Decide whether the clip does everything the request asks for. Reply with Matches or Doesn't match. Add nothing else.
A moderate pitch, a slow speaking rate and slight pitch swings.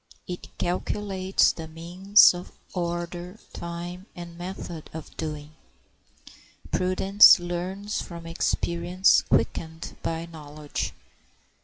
Matches